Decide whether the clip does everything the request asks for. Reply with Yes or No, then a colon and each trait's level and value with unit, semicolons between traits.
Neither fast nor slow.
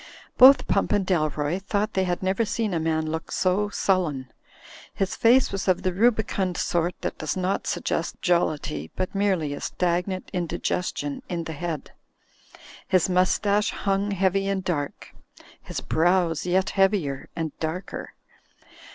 Yes: average, 150 wpm